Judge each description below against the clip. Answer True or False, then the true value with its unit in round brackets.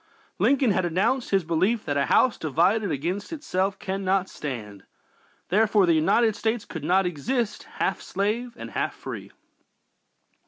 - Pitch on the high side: True (195 Hz)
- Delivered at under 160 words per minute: True (150 wpm)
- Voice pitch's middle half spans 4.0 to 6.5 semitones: True (4.8 semitones)